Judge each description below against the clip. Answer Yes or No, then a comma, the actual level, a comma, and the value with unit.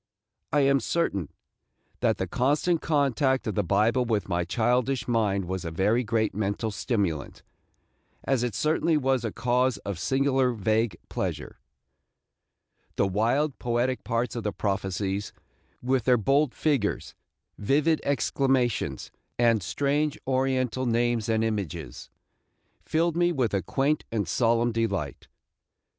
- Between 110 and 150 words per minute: Yes, slow, 135 wpm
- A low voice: Yes, low, 120 Hz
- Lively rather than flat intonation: No, average, 4.5 semitones